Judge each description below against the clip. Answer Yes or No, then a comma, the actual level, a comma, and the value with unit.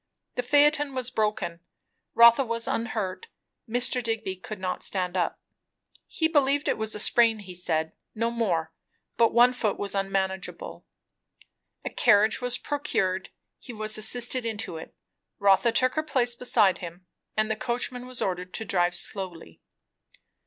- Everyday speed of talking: Yes, average, 150 wpm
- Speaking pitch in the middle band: No, high, 220 Hz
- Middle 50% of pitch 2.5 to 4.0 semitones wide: No, average, 4.5 semitones